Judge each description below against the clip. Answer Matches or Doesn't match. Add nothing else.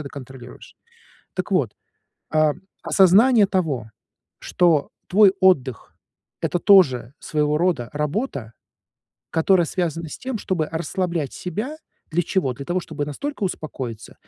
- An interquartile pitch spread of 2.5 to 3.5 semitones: Doesn't match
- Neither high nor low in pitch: Matches